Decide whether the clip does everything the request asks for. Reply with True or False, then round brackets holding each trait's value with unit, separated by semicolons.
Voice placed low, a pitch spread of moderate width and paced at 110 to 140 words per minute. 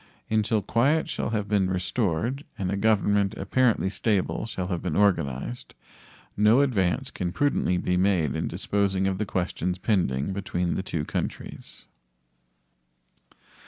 True (95 Hz; 3.0 semitones; 135 wpm)